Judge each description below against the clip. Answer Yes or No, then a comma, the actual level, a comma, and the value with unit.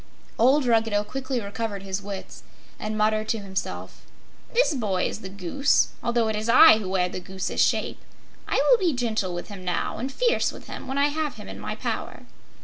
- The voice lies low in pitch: No, high, 220 Hz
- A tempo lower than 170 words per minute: No, average, 200 wpm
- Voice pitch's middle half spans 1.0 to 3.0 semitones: No, average, 5.1 semitones